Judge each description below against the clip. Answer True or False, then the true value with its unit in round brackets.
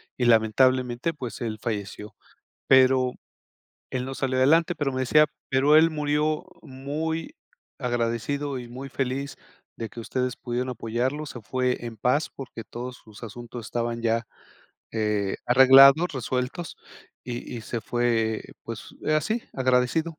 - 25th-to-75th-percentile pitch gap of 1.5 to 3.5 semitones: True (2.9 semitones)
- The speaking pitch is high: False (130 Hz)